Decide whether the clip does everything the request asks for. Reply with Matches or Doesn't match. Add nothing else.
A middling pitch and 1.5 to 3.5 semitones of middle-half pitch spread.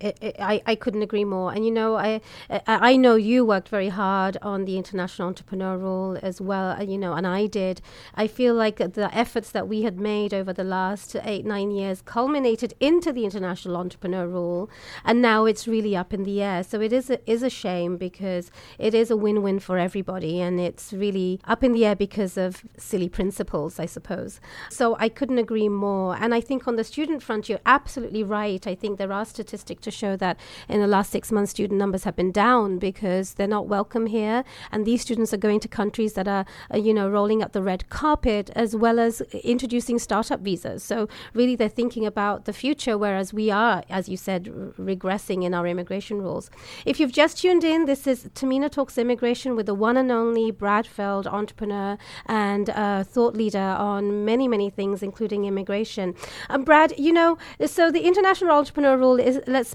Doesn't match